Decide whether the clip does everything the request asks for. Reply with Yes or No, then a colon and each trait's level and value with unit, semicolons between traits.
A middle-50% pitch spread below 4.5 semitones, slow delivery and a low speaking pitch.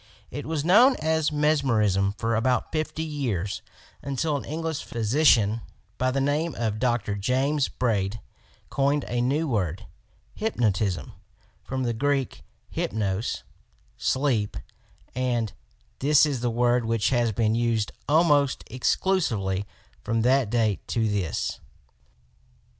No: average, 4.9 semitones; slow, 125 wpm; low, 125 Hz